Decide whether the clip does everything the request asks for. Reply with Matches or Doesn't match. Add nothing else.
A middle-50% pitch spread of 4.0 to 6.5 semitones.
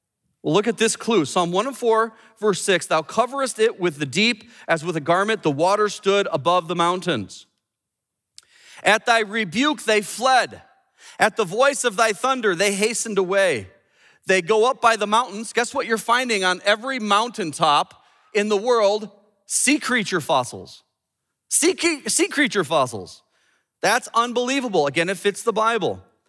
Doesn't match